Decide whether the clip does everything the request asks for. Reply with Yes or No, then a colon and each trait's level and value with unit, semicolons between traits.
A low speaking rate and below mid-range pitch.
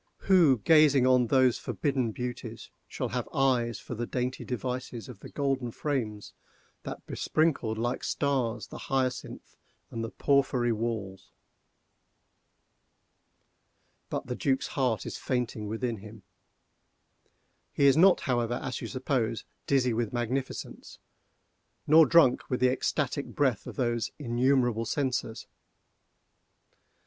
Yes: slow, 120 wpm; low, 125 Hz